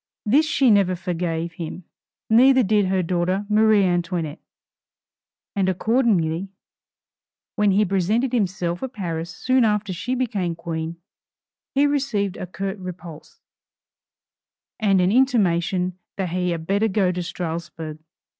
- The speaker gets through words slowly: Yes, slow, 125 wpm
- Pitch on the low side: No, high, 190 Hz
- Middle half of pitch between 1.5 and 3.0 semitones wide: No, average, 3.8 semitones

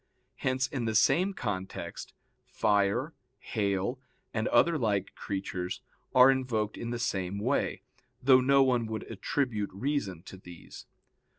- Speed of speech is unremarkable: No, slow, 130 wpm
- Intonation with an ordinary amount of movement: Yes, average, 4.6 semitones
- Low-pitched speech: Yes, low, 110 Hz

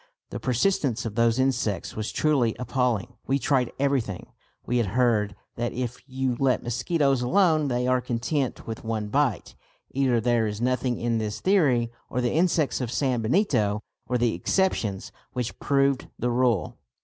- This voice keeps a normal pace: Yes, average, 160 wpm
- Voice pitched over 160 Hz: No, low, 125 Hz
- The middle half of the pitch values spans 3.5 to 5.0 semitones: No, average, 2.9 semitones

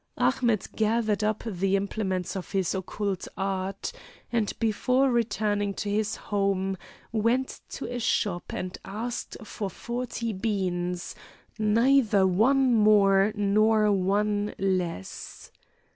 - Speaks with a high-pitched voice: Yes, high, 205 Hz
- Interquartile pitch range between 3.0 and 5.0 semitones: No, narrow, 2.5 semitones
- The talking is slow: Yes, slow, 115 wpm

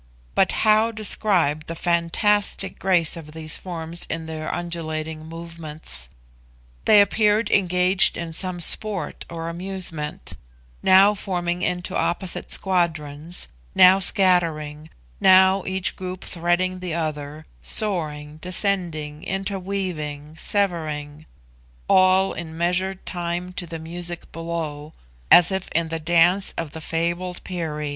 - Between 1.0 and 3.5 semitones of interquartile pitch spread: Yes, average, 2.8 semitones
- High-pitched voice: No, medium, 175 Hz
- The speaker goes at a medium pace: No, slow, 120 wpm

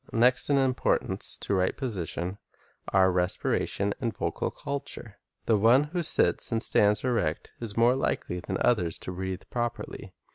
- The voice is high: No, low, 110 Hz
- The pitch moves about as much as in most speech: Yes, average, 4.7 semitones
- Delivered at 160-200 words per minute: No, average, 150 wpm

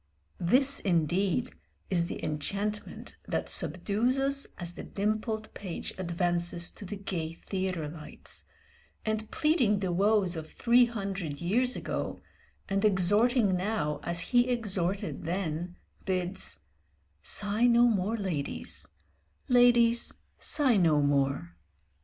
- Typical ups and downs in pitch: Yes, average, 4.5 semitones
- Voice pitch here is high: Yes, high, 195 Hz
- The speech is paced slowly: Yes, slow, 115 wpm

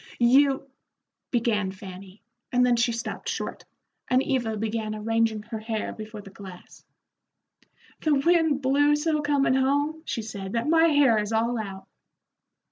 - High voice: Yes, high, 235 Hz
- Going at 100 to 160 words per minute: Yes, average, 150 wpm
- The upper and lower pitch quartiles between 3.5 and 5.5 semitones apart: Yes, average, 4.7 semitones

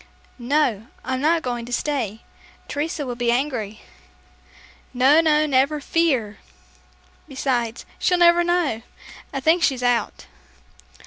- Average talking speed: No, slow, 120 wpm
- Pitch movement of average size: Yes, average, 4.3 semitones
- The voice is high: Yes, very high, 265 Hz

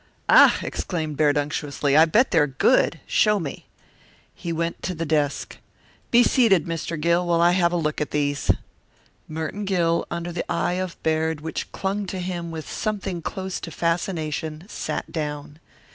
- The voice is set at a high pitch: No, medium, 165 Hz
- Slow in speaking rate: No, average, 165 wpm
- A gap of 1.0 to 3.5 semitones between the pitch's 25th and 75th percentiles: Yes, average, 2.9 semitones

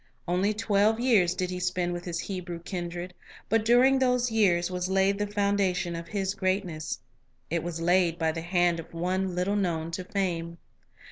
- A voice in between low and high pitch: Yes, medium, 180 Hz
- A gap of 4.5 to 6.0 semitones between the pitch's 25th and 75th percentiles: No, average, 2.7 semitones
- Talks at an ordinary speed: Yes, average, 180 wpm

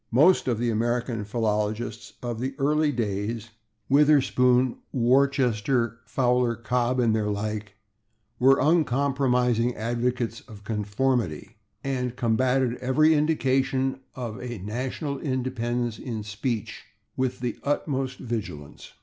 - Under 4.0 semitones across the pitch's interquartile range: Yes, average, 2.8 semitones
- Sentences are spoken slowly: Yes, slow, 110 wpm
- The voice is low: Yes, low, 125 Hz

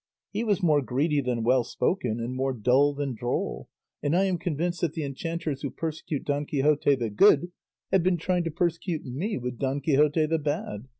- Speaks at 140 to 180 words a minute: No, average, 195 wpm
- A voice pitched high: No, medium, 145 Hz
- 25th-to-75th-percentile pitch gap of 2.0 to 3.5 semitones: No, average, 4.2 semitones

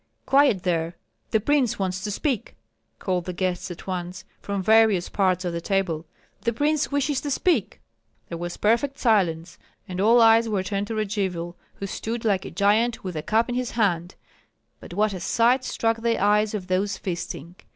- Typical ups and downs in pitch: Yes, average, 3.9 semitones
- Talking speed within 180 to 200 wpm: Yes, average, 185 wpm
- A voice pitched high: Yes, high, 200 Hz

